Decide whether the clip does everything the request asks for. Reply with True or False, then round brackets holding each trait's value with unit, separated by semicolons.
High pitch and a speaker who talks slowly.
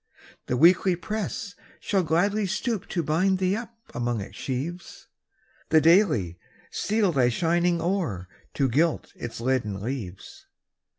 False (165 Hz; 130 wpm)